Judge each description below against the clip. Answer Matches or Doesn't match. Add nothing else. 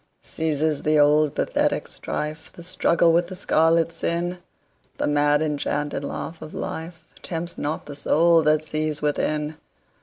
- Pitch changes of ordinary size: Doesn't match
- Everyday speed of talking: Doesn't match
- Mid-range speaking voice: Matches